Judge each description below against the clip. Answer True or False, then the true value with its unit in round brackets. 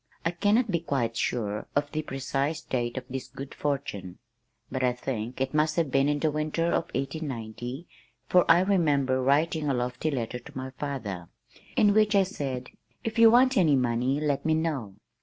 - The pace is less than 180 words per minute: False (185 wpm)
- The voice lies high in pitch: False (140 Hz)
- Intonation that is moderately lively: True (4.2 semitones)